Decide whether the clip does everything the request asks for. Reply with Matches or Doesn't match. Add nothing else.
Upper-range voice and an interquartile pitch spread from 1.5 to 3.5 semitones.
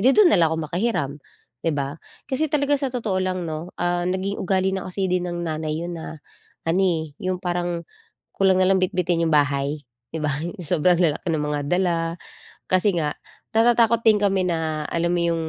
Doesn't match